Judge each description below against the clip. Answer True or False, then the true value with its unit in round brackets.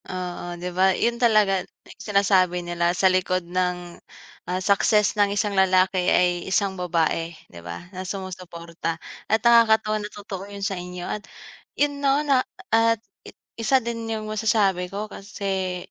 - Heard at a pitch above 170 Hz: True (190 Hz)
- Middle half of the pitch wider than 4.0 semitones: False (3.0 semitones)